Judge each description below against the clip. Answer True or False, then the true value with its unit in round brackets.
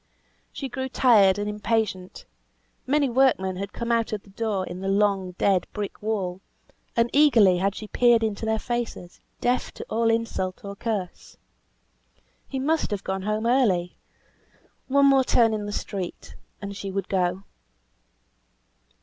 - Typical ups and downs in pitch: True (3.5 semitones)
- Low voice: False (210 Hz)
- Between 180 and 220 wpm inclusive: False (155 wpm)